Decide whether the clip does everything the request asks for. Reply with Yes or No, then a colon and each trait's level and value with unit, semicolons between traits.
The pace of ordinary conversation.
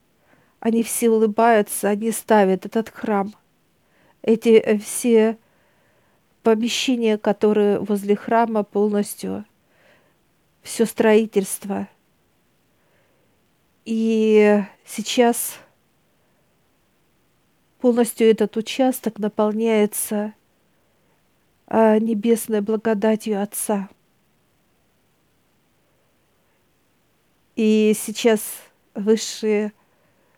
No: slow, 55 wpm